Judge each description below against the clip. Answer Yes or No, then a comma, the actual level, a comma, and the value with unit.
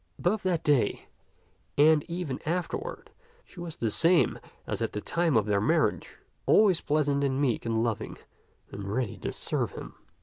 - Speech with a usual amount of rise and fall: No, wide, 7.0 semitones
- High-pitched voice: No, medium, 145 Hz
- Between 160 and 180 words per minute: Yes, average, 165 wpm